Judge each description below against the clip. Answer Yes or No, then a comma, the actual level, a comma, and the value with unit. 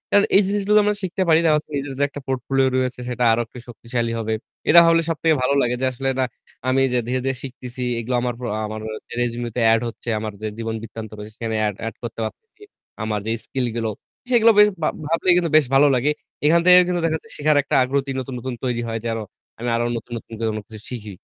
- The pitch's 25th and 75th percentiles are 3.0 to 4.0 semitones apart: No, average, 5.1 semitones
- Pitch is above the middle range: No, low, 125 Hz